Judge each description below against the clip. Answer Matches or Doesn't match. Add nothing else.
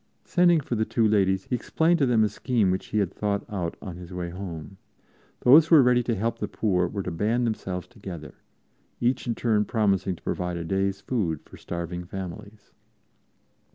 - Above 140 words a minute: Matches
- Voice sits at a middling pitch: Doesn't match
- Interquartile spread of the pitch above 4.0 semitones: Matches